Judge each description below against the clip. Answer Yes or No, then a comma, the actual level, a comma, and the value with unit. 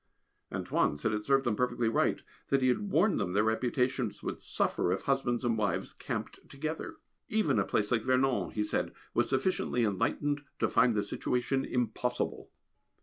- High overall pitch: No, low, 125 Hz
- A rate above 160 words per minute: Yes, average, 170 wpm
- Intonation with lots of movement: No, average, 3.5 semitones